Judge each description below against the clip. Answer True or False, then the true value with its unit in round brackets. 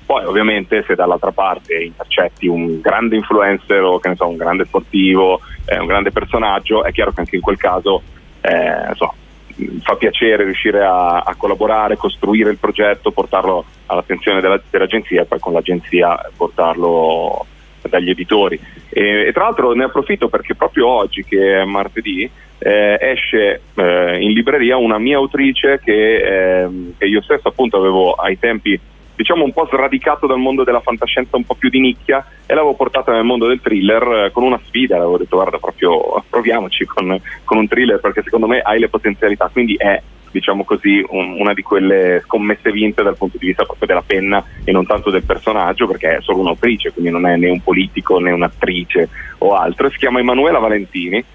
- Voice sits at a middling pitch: False (100 Hz)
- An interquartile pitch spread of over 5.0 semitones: False (4.7 semitones)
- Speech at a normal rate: False (185 wpm)